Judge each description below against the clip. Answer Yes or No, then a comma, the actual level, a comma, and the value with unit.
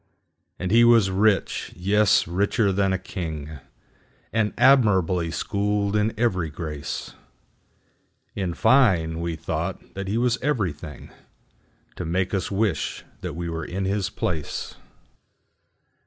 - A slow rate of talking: Yes, slow, 110 wpm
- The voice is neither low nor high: No, very low, 95 Hz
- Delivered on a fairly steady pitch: No, average, 4.0 semitones